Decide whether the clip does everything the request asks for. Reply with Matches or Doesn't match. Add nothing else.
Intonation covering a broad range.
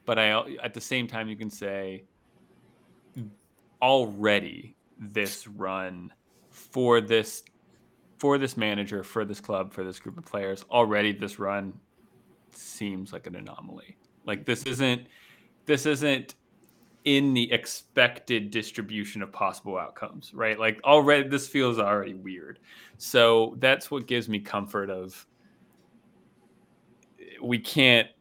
Doesn't match